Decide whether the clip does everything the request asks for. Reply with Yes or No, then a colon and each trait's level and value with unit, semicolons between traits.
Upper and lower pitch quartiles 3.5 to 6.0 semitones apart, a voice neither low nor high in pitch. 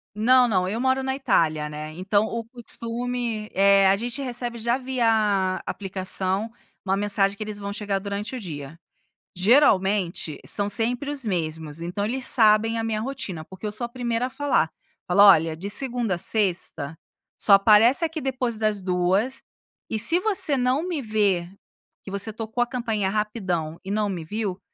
No: average, 4.0 semitones; high, 210 Hz